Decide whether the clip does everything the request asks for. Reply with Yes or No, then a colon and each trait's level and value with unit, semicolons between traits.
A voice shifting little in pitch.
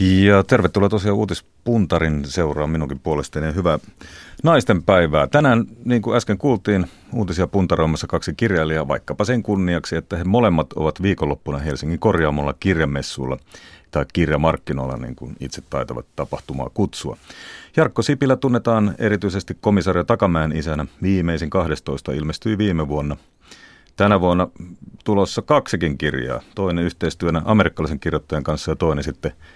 No: average, 5.1 semitones